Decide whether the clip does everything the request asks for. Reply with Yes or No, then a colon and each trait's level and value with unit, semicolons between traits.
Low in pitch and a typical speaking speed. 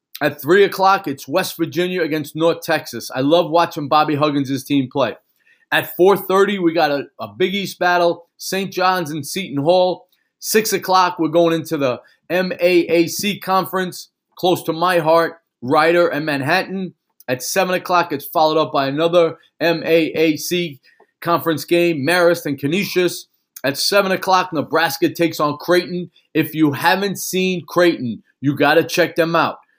No: medium, 170 Hz; average, 155 wpm